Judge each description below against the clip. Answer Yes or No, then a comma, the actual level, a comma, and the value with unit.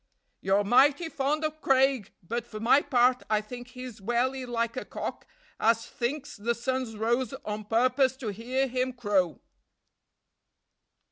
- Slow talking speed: No, average, 145 wpm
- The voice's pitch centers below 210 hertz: No, high, 245 Hz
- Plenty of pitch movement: No, average, 2.7 semitones